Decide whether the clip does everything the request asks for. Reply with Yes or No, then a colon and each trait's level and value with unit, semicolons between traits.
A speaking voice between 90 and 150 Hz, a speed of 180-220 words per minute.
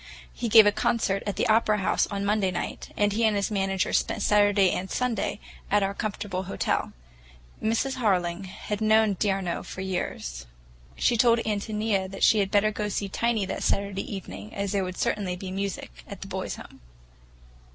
No: high, 200 Hz; average, 185 wpm